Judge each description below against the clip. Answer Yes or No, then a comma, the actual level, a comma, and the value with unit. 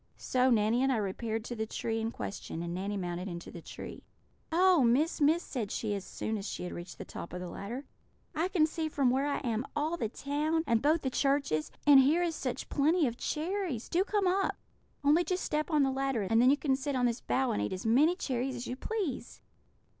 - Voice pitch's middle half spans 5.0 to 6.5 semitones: Yes, wide, 5.6 semitones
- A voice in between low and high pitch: No, very high, 265 Hz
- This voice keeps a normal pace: No, fast, 235 wpm